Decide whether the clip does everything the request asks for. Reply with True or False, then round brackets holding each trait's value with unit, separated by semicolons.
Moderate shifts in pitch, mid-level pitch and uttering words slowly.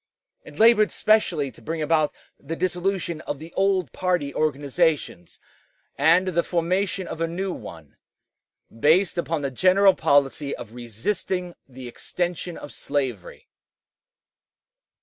True (4.6 semitones; 165 Hz; 125 wpm)